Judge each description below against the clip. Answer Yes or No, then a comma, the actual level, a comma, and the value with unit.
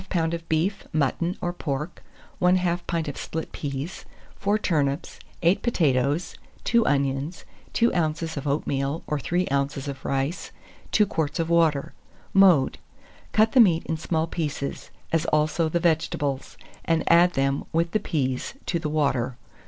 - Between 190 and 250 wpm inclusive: No, average, 150 wpm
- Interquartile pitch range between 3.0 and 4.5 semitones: Yes, average, 3.7 semitones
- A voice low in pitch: No, medium, 160 Hz